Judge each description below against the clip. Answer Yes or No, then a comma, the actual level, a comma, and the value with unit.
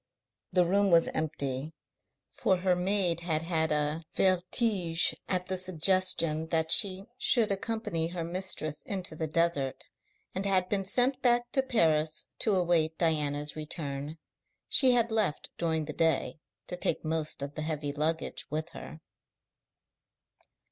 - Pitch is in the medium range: Yes, medium, 170 Hz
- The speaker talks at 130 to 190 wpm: Yes, average, 140 wpm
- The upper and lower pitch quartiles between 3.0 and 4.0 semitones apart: Yes, average, 3.4 semitones